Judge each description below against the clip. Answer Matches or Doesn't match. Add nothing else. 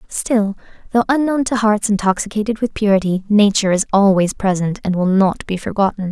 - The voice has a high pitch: Matches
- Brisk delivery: Doesn't match